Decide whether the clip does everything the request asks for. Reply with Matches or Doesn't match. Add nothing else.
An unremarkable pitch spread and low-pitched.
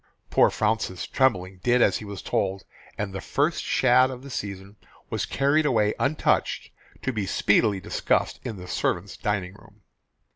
Matches